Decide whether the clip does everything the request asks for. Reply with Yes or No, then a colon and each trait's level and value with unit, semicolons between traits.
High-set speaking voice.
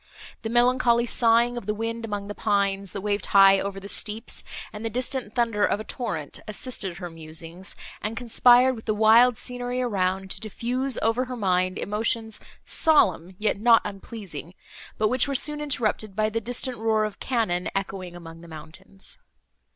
Yes: high, 215 Hz